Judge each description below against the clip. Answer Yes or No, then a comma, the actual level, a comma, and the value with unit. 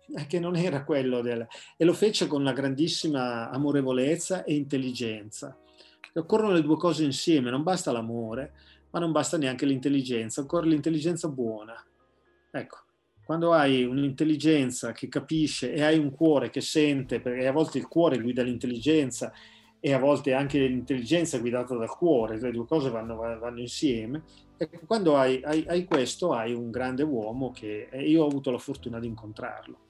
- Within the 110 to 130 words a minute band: No, average, 165 wpm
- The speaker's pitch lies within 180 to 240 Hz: No, low, 135 Hz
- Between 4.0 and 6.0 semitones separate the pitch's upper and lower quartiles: Yes, average, 4.3 semitones